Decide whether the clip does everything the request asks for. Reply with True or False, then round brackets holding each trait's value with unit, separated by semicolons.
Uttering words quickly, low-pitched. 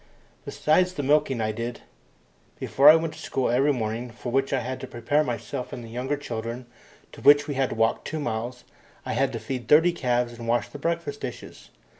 True (215 wpm; 130 Hz)